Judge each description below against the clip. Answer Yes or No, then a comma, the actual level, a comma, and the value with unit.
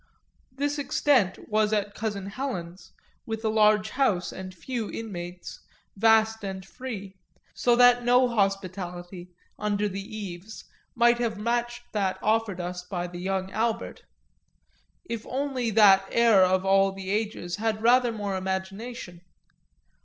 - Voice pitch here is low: No, high, 210 Hz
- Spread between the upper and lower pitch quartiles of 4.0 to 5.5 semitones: No, average, 3.6 semitones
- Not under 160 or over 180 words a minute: No, average, 140 wpm